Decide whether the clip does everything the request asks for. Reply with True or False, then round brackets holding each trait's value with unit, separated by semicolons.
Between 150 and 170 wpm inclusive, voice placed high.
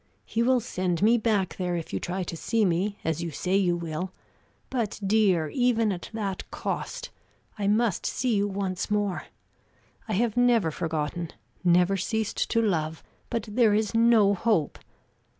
True (165 wpm; 200 Hz)